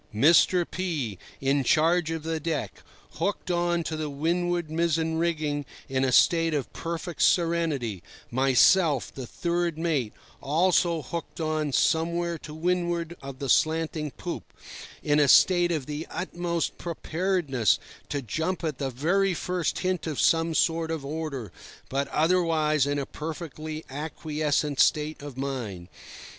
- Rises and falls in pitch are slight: No, average, 3.0 semitones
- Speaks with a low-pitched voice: No, medium, 160 Hz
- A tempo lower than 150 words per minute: Yes, average, 140 wpm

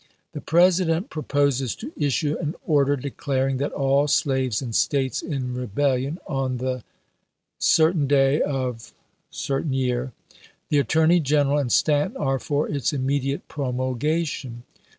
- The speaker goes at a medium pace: No, slow, 125 wpm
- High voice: No, medium, 140 Hz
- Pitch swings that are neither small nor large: No, narrow, 2.3 semitones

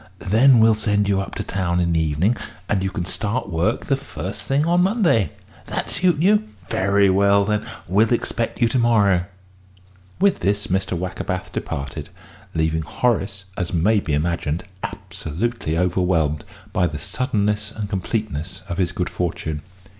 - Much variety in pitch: No, average, 4.3 semitones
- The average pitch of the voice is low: Yes, low, 100 Hz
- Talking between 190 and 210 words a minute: No, average, 160 wpm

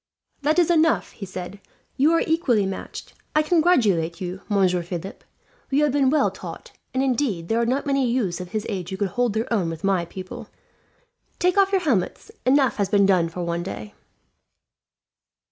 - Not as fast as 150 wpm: No, average, 185 wpm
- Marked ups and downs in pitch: Yes, wide, 7.5 semitones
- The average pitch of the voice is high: Yes, high, 215 Hz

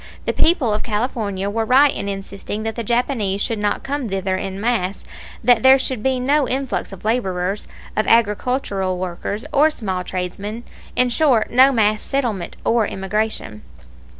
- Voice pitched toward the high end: Yes, high, 220 Hz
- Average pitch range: Yes, average, 4.3 semitones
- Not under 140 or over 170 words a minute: Yes, average, 160 wpm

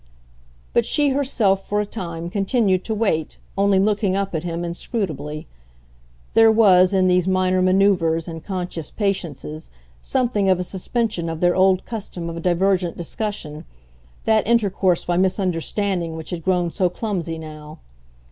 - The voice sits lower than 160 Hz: No, medium, 185 Hz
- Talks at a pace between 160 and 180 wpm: No, average, 145 wpm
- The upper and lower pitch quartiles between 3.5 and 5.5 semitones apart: No, average, 3.1 semitones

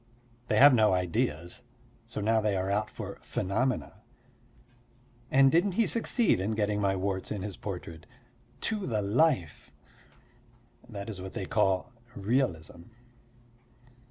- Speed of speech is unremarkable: No, slow, 130 wpm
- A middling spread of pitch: Yes, average, 4.9 semitones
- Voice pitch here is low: Yes, low, 105 Hz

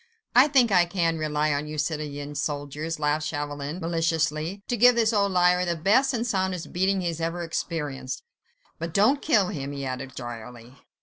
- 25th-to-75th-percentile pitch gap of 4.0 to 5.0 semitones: Yes, average, 4.5 semitones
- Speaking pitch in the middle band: Yes, medium, 165 Hz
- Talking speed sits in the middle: Yes, average, 180 wpm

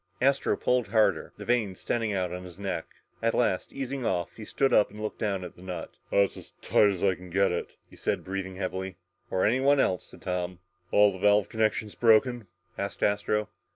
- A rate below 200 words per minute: No, fast, 205 wpm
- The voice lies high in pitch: No, low, 100 Hz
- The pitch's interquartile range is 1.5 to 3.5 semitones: Yes, average, 3.1 semitones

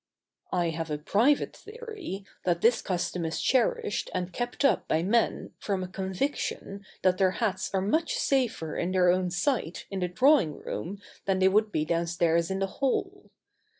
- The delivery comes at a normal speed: Yes, average, 175 wpm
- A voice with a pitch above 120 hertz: Yes, high, 190 Hz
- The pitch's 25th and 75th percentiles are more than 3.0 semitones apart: Yes, average, 5.0 semitones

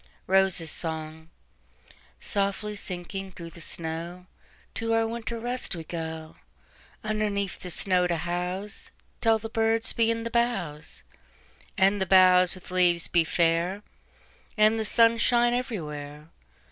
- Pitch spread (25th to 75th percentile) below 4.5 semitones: No, average, 5.1 semitones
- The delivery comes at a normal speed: No, slow, 110 wpm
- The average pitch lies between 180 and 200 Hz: Yes, medium, 185 Hz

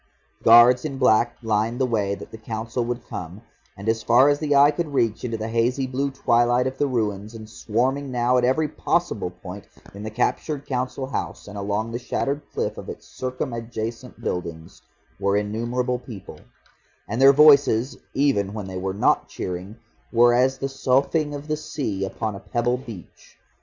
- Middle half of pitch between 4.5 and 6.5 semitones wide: No, average, 3.7 semitones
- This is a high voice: No, low, 120 Hz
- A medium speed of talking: Yes, average, 180 wpm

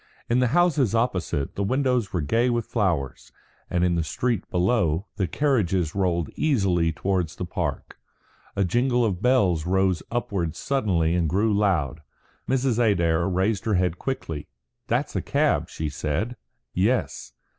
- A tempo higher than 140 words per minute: Yes, average, 150 wpm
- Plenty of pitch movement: Yes, wide, 5.9 semitones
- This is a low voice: Yes, very low, 95 Hz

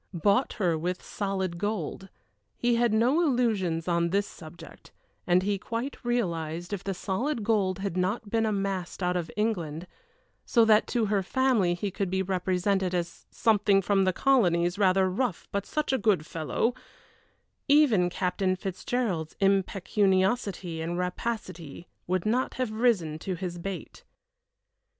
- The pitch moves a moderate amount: Yes, average, 3.8 semitones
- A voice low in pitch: No, high, 195 Hz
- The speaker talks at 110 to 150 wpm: Yes, average, 145 wpm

